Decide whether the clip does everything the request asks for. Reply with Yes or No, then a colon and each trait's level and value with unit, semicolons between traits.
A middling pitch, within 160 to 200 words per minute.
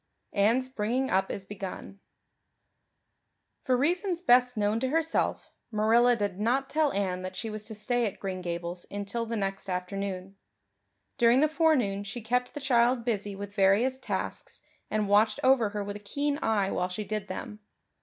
No: high, 215 Hz; average, 170 wpm